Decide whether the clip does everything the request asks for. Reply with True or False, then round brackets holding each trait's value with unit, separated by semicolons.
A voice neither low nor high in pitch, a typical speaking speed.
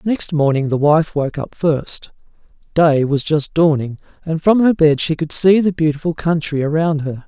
True (155 Hz; 190 wpm)